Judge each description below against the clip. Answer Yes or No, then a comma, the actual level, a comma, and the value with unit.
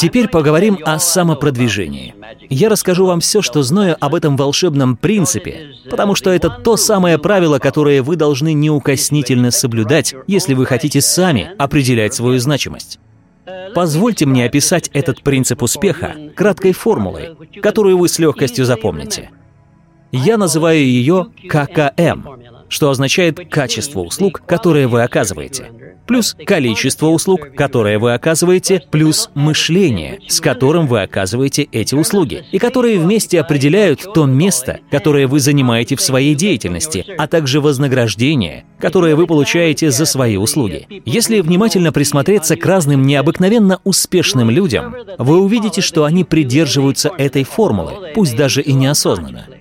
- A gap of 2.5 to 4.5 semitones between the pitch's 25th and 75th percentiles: No, average, 4.9 semitones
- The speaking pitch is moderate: Yes, medium, 150 Hz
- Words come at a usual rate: Yes, average, 135 wpm